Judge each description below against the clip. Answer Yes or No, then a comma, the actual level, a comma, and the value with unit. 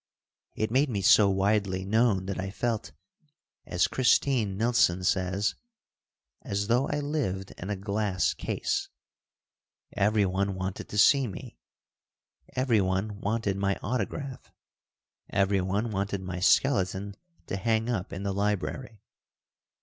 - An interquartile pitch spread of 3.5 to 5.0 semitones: No, average, 3.0 semitones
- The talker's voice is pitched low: Yes, low, 100 Hz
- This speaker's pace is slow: Yes, slow, 120 wpm